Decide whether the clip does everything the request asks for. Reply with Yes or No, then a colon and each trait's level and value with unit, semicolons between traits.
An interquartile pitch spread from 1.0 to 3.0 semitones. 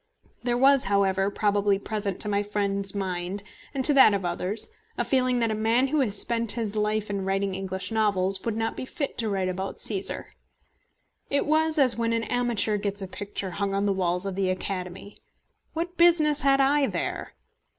No: average, 4.0 semitones